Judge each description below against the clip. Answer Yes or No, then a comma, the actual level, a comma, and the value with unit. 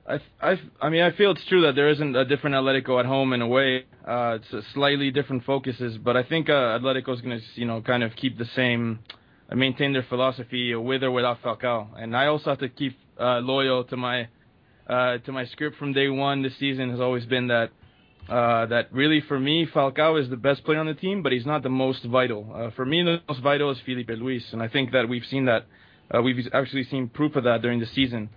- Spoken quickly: Yes, fast, 245 wpm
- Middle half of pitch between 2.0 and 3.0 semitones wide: Yes, narrow, 2.5 semitones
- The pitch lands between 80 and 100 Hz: No, low, 130 Hz